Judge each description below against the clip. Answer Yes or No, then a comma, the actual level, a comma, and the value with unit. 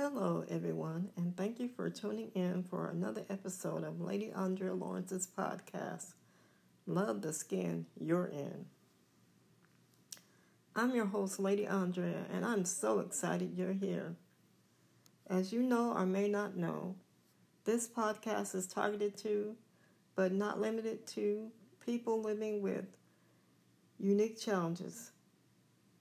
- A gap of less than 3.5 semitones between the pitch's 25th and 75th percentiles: Yes, narrow, 2.5 semitones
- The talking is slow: Yes, slow, 120 wpm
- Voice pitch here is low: No, high, 195 Hz